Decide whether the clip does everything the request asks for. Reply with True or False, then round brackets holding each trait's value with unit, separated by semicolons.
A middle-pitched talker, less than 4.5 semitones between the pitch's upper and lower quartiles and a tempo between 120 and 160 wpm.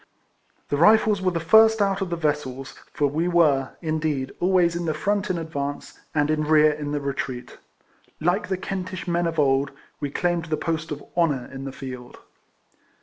False (155 Hz; 3.6 semitones; 185 wpm)